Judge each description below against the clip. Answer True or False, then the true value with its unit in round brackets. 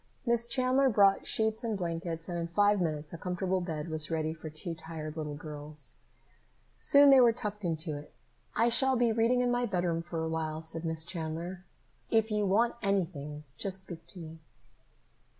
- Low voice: False (175 Hz)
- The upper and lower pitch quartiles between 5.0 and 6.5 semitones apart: True (5.4 semitones)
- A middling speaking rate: True (185 wpm)